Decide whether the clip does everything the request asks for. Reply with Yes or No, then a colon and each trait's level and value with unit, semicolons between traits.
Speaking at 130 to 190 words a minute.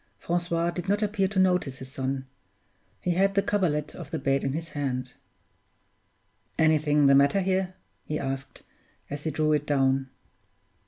Yes: average, 160 wpm